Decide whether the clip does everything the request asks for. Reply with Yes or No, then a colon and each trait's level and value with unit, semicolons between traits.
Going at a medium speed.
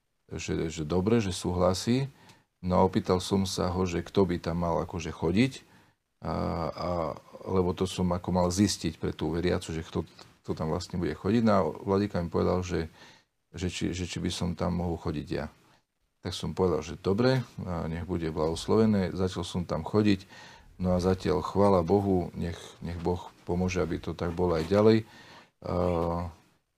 No: fast, 180 wpm